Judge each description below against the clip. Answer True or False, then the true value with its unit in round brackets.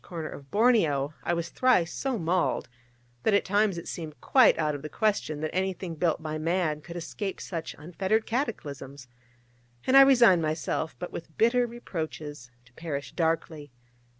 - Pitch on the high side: False (170 Hz)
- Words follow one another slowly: False (165 wpm)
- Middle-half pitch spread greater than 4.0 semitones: True (5.0 semitones)